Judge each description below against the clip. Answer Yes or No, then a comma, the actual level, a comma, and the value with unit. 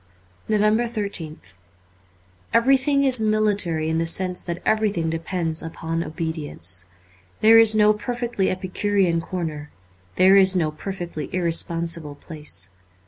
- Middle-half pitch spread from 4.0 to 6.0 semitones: Yes, average, 4.7 semitones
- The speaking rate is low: Yes, slow, 120 wpm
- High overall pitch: No, medium, 180 Hz